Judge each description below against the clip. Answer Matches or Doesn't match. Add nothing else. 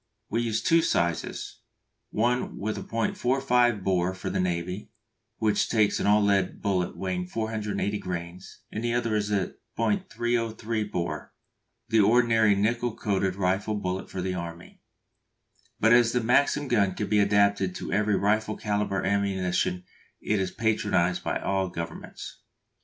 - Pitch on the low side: Matches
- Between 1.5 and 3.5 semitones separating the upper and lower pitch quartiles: Matches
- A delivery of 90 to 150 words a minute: Matches